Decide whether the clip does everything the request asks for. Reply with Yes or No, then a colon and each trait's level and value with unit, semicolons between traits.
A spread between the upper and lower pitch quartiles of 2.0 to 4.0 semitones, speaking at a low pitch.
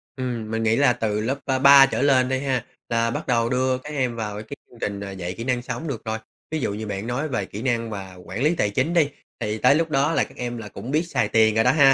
Yes: average, 3.6 semitones; low, 125 Hz